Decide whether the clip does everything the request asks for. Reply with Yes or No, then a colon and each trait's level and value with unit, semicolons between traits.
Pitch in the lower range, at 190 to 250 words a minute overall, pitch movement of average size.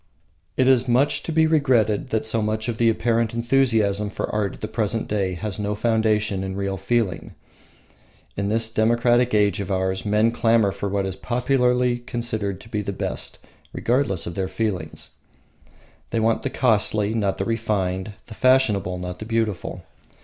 No: low, 110 Hz; average, 165 wpm; average, 3.0 semitones